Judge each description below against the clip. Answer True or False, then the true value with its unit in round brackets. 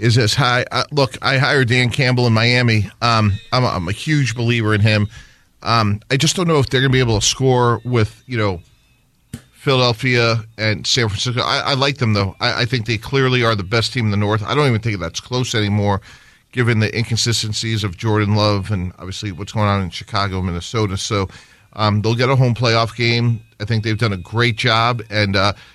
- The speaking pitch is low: True (115 Hz)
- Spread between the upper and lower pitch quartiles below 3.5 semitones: True (2.9 semitones)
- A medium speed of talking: False (225 wpm)